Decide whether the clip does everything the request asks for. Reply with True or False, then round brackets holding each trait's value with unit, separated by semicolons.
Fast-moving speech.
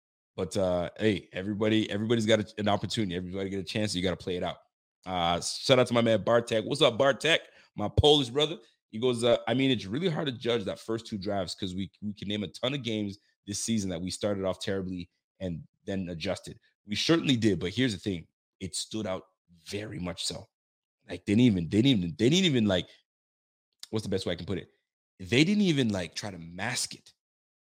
True (230 wpm)